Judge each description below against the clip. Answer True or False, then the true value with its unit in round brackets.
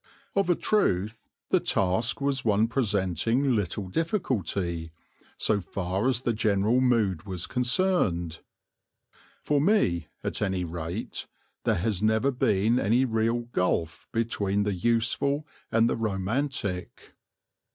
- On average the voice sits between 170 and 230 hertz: False (110 Hz)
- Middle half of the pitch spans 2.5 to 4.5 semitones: False (4.9 semitones)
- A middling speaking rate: False (120 wpm)